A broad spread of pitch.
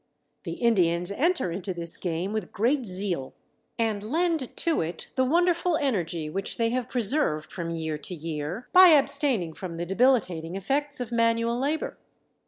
Yes: wide, 7.8 semitones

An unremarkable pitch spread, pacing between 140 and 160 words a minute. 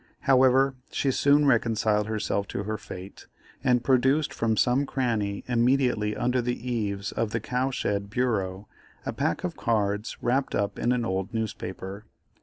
Yes: average, 3.7 semitones; average, 155 wpm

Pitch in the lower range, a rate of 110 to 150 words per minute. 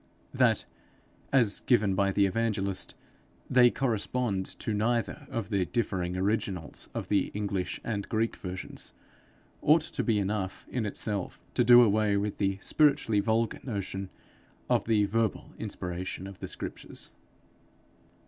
Yes: low, 105 Hz; slow, 135 wpm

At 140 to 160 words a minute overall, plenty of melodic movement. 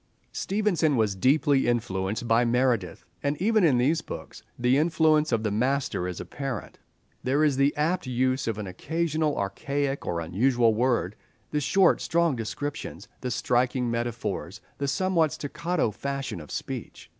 No: average, 150 wpm; average, 4.8 semitones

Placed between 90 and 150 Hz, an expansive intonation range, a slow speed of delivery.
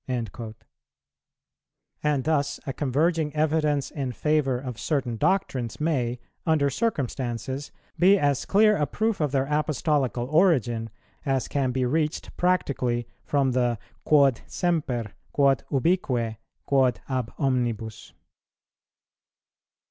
No: medium, 140 Hz; average, 3.8 semitones; slow, 110 wpm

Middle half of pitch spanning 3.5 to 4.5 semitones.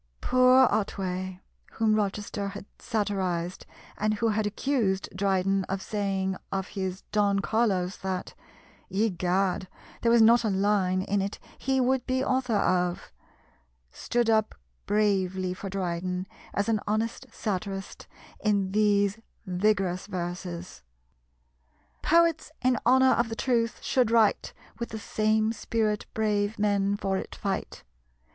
No: average, 2.9 semitones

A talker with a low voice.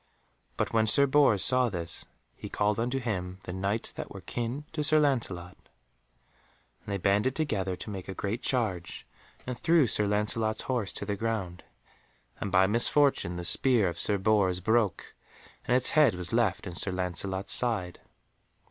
Yes: low, 105 Hz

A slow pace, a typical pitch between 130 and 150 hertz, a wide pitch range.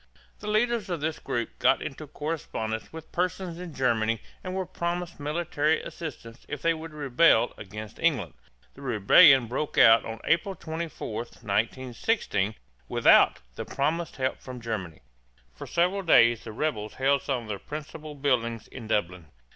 No: average, 150 wpm; medium, 140 Hz; wide, 6.4 semitones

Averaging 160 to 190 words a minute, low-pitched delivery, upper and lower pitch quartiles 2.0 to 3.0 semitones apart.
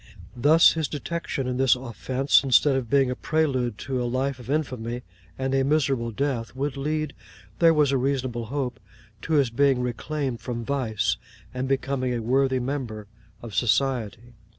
Yes: average, 165 wpm; low, 130 Hz; narrow, 2.5 semitones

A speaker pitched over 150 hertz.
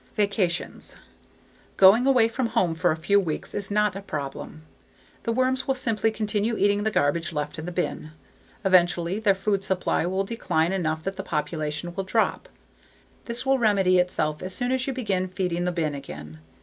Yes: high, 190 Hz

